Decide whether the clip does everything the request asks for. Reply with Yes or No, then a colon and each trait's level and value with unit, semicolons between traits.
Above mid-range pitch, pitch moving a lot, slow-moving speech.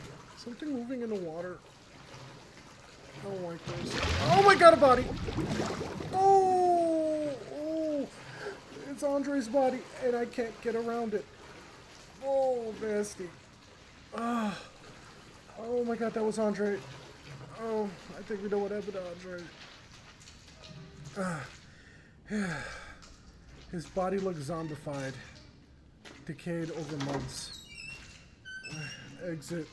Yes: high, 210 Hz; wide, 7.3 semitones; slow, 105 wpm